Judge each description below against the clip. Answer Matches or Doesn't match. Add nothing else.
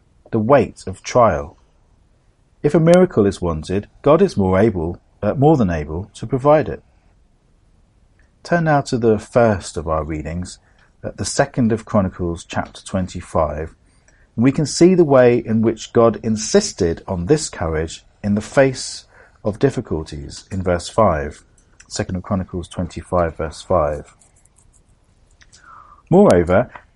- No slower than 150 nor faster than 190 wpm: Doesn't match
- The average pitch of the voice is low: Matches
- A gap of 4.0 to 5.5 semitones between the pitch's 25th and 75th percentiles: Matches